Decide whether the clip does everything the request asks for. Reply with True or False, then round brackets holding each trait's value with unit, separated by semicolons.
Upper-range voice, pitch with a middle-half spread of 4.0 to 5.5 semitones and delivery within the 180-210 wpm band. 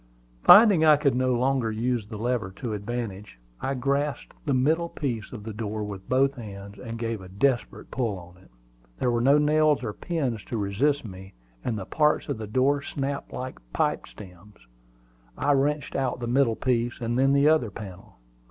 False (120 Hz; 4.6 semitones; 190 wpm)